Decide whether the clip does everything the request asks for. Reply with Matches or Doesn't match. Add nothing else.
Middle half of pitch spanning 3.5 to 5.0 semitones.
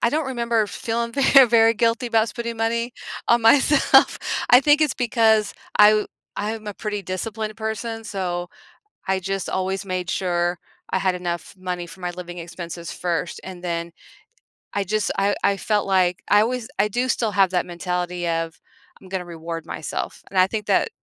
Matches